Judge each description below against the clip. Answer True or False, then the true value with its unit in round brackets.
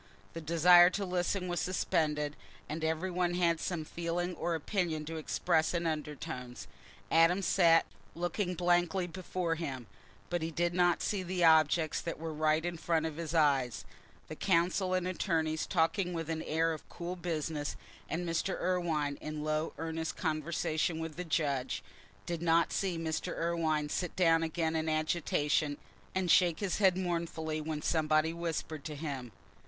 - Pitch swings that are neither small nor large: False (2.1 semitones)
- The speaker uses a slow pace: False (160 wpm)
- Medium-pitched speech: True (165 Hz)